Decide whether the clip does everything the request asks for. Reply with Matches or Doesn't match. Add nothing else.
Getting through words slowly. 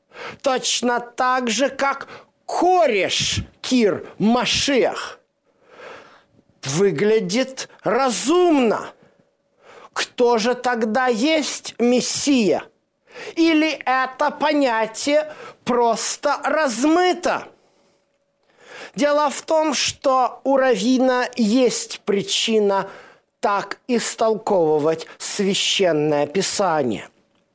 Matches